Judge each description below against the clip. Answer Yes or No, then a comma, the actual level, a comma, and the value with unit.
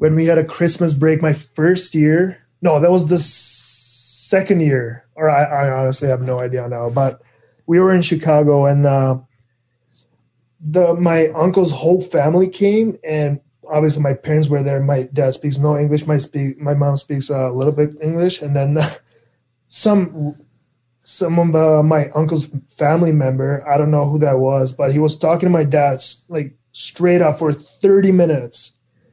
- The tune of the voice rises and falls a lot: No, average, 3.5 semitones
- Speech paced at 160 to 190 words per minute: Yes, average, 170 wpm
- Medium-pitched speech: Yes, medium, 145 Hz